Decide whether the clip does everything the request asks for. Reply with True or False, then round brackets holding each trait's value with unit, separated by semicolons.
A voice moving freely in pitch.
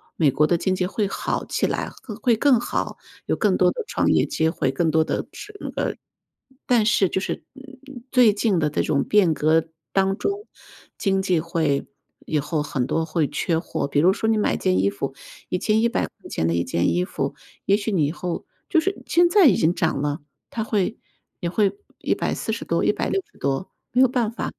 True (6.5 semitones)